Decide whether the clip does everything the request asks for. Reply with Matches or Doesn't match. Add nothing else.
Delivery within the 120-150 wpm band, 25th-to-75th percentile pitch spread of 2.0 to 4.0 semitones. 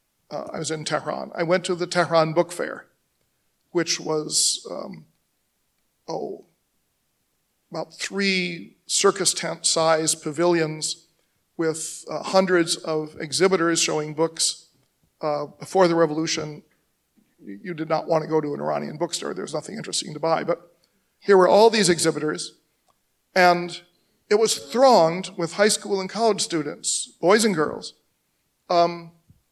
Matches